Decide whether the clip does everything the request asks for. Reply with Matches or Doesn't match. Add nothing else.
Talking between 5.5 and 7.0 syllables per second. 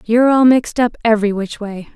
Matches